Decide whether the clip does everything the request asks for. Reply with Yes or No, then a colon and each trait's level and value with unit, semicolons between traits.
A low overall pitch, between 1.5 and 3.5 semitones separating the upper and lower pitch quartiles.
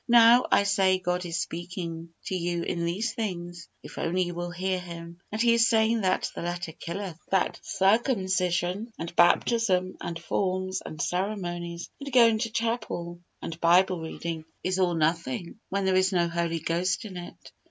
No: medium, 180 Hz; average, 2.7 semitones